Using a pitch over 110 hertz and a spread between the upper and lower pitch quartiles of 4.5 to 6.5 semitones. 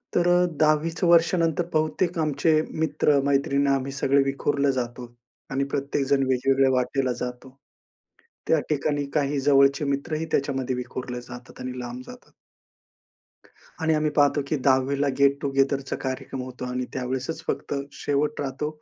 No: medium, 140 Hz; narrow, 2.5 semitones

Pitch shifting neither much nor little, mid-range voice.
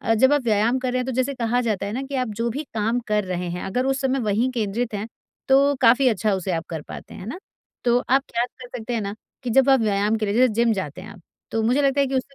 No: average, 3.8 semitones; high, 235 Hz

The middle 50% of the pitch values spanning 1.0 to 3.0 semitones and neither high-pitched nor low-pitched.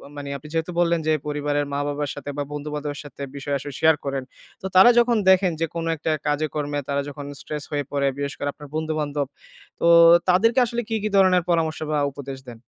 Yes: narrow, 2.5 semitones; medium, 150 Hz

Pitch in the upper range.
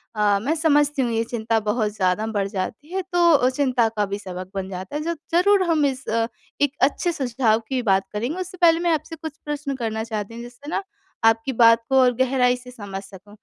Yes: high, 245 Hz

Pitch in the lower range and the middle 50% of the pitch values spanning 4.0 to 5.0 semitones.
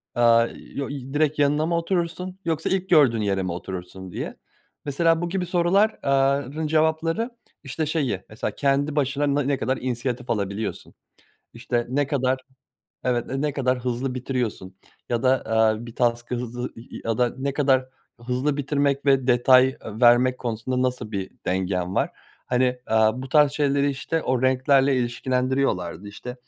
No: low, 130 Hz; average, 3.3 semitones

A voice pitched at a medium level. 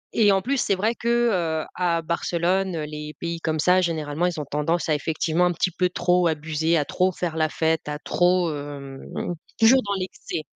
Yes: medium, 170 Hz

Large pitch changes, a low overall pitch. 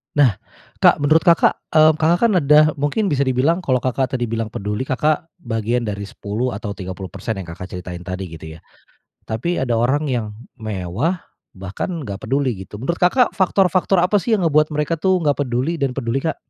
Yes: wide, 6.7 semitones; low, 130 Hz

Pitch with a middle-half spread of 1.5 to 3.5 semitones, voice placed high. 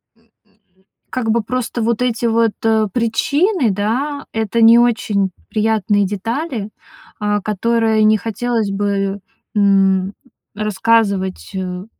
Yes: narrow, 2.5 semitones; high, 220 Hz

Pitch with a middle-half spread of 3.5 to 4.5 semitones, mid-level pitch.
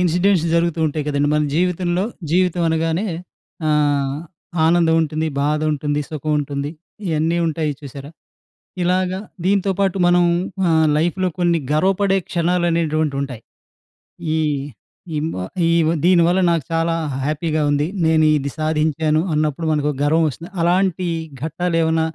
No: narrow, 2.5 semitones; medium, 160 Hz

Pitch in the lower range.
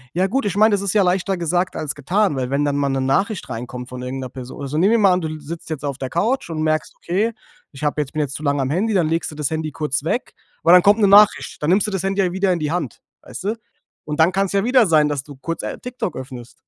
No: medium, 160 Hz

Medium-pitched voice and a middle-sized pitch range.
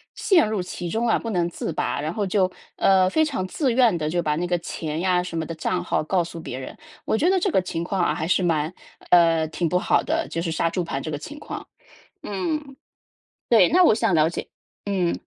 Yes: medium, 180 Hz; average, 4.7 semitones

